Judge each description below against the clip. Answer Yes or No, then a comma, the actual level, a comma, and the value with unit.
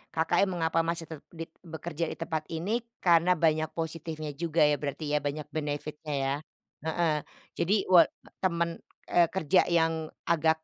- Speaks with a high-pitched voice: No, medium, 160 Hz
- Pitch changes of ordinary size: No, narrow, 1.7 semitones